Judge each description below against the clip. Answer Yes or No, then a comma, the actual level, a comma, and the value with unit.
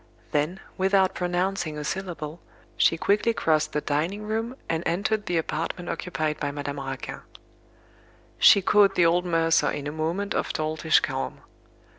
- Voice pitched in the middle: Yes, medium, 165 Hz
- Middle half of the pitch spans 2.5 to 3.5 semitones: No, average, 3.9 semitones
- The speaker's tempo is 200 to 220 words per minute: No, average, 150 wpm